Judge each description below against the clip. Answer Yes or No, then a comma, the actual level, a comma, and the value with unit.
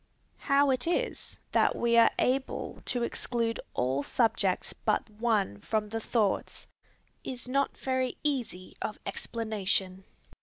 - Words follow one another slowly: Yes, slow, 125 wpm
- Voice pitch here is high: Yes, high, 230 Hz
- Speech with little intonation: No, average, 3.7 semitones